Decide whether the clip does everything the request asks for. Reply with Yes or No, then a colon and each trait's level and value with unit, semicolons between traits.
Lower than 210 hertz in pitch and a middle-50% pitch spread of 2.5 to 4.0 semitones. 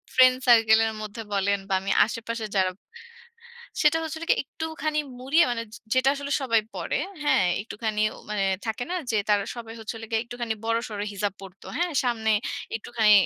No: high, 230 Hz; average, 3.3 semitones